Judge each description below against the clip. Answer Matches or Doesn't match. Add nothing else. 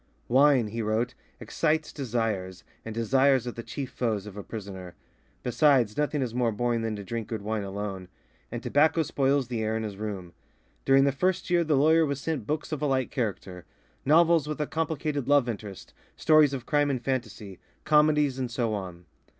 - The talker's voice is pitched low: Matches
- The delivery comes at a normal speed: Matches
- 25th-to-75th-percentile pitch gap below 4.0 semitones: Doesn't match